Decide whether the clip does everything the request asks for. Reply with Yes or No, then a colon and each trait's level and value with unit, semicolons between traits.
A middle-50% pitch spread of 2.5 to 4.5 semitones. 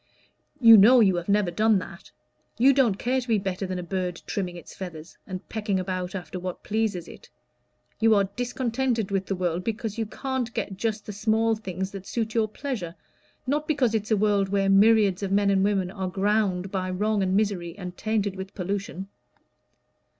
Yes: average, 2.9 semitones